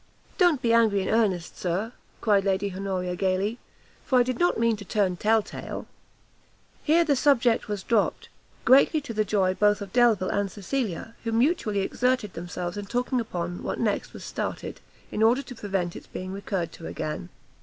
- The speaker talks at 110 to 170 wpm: No, average, 180 wpm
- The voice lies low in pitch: No, high, 210 Hz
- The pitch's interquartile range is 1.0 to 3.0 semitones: No, average, 4.1 semitones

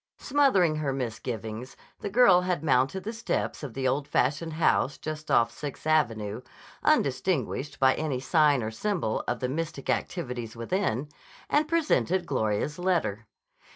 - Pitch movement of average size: No, wide, 6.2 semitones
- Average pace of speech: Yes, average, 145 wpm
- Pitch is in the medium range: Yes, medium, 145 Hz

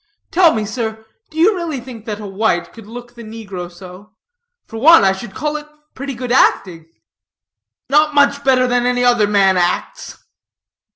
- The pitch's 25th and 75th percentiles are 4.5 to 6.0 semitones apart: Yes, average, 5.3 semitones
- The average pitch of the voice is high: Yes, high, 235 Hz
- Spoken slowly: No, average, 175 wpm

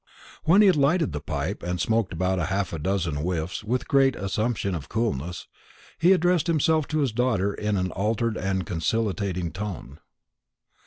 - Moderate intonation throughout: No, wide, 6.0 semitones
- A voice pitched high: No, low, 100 Hz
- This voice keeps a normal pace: Yes, average, 170 wpm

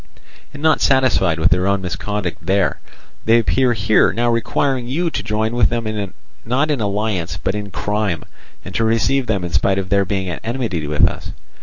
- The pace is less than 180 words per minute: No, average, 190 wpm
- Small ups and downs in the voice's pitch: No, average, 3.8 semitones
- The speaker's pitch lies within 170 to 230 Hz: No, low, 105 Hz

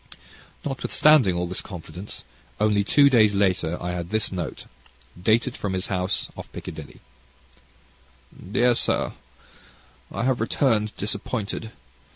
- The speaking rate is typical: No, slow, 120 wpm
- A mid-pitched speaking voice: No, low, 105 Hz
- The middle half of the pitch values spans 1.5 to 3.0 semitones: No, average, 4.3 semitones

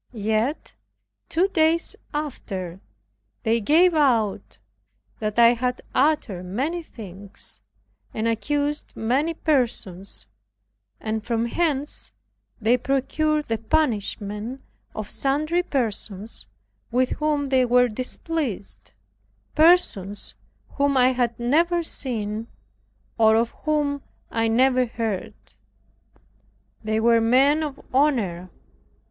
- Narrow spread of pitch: No, average, 5.2 semitones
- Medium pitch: No, very high, 250 Hz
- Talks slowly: Yes, slow, 100 wpm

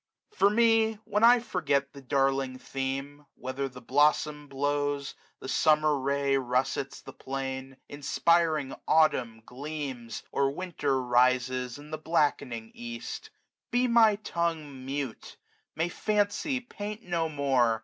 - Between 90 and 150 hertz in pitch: Yes, medium, 140 Hz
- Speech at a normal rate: No, slow, 130 wpm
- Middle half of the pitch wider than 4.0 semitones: No, average, 3.7 semitones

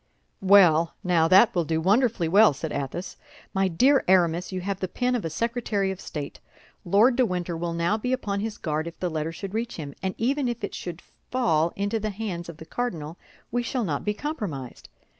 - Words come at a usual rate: No, fast, 210 wpm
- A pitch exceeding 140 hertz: Yes, high, 190 Hz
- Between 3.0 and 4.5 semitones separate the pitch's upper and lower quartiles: No, average, 5.2 semitones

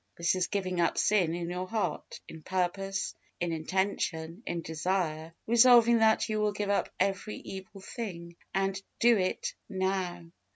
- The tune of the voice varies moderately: Yes, average, 3.1 semitones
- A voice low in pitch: No, high, 190 Hz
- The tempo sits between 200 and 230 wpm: No, average, 155 wpm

